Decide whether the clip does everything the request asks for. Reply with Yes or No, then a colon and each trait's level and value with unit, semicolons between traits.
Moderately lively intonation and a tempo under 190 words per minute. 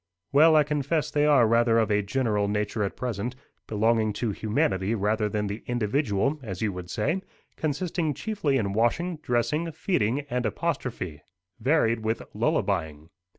No: wide, 5.9 semitones; average, 150 wpm